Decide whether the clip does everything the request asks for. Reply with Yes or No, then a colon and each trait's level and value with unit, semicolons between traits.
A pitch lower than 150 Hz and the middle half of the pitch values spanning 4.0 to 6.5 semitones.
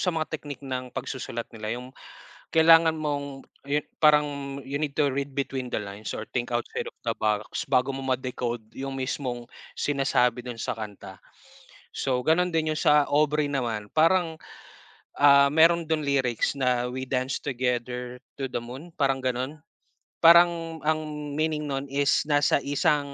No: low, 135 Hz; average, 3.4 semitones